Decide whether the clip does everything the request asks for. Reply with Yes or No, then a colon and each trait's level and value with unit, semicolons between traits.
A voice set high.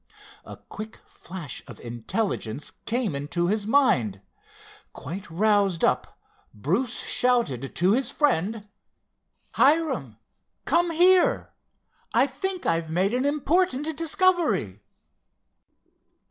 Yes: high, 220 Hz